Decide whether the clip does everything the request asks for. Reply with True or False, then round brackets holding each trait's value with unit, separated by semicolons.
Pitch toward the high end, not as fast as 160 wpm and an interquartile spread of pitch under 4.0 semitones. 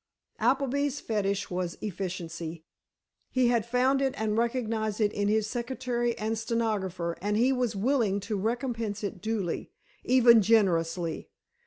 True (220 Hz; 135 wpm; 3.6 semitones)